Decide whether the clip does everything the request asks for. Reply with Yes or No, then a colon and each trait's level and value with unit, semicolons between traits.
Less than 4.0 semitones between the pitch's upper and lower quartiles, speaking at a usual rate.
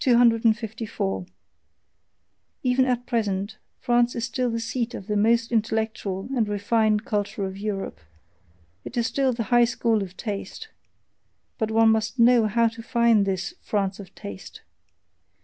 Yes: narrow, 2.5 semitones; average, 145 wpm